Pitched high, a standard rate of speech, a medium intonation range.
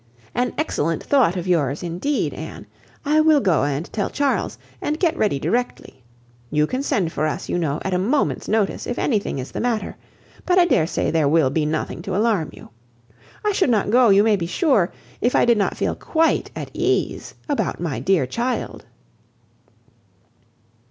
No: high, 200 Hz; average, 185 wpm; wide, 7.9 semitones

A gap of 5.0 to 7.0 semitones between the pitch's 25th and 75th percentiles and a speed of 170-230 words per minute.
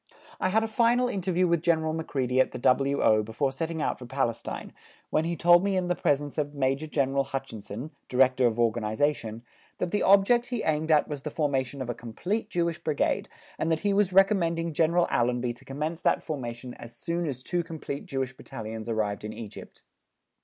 Yes: average, 5.3 semitones; average, 190 wpm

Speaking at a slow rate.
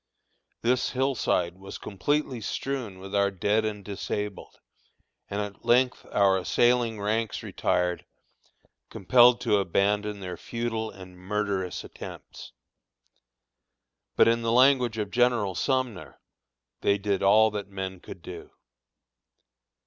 Yes: slow, 120 wpm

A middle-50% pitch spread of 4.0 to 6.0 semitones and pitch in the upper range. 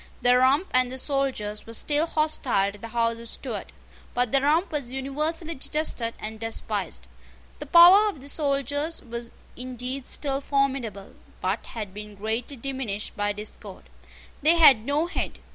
Yes: average, 4.4 semitones; very high, 255 Hz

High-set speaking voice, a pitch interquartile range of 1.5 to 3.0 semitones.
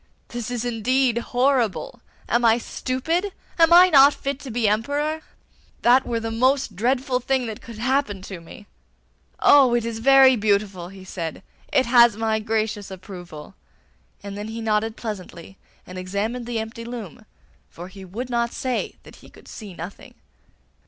No: high, 230 Hz; average, 3.8 semitones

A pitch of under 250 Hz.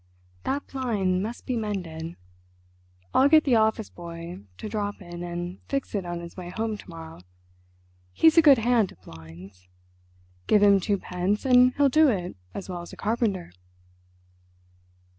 Yes: high, 190 Hz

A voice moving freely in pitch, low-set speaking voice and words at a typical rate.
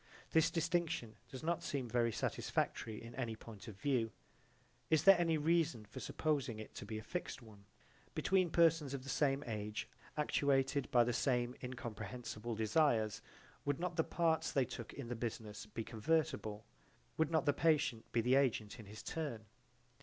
Yes: wide, 5.8 semitones; low, 125 Hz; average, 170 wpm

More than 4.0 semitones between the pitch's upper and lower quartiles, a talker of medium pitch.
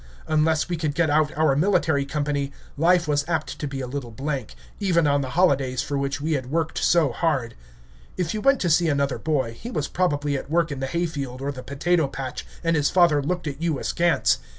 No: average, 3.2 semitones; medium, 150 Hz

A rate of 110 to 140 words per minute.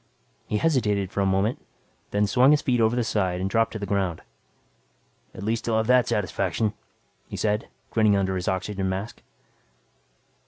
No: average, 170 wpm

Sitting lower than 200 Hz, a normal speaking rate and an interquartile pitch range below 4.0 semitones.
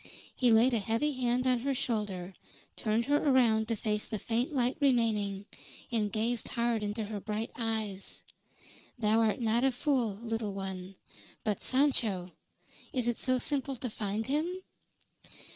No: high, 230 Hz; average, 155 wpm; average, 3.1 semitones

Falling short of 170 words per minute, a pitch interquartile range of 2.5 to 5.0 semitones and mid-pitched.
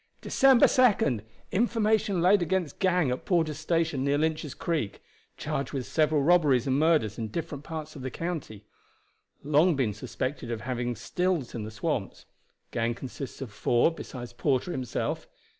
No: average, 155 wpm; wide, 5.5 semitones; medium, 150 Hz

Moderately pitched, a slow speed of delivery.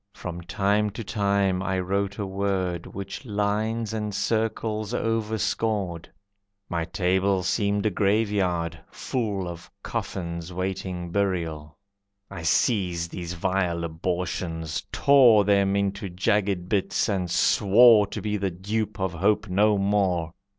No: very low, 95 Hz; slow, 125 wpm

